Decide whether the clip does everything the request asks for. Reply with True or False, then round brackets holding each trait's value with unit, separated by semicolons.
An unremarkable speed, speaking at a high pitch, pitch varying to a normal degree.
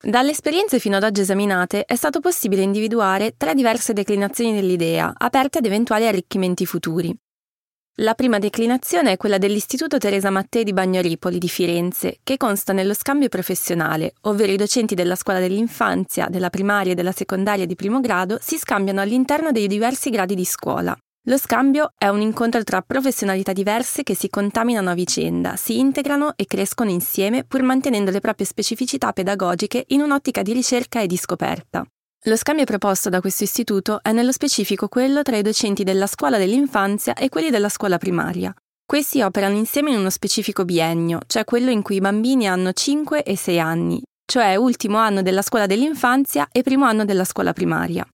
False (175 wpm; 210 Hz; 4.5 semitones)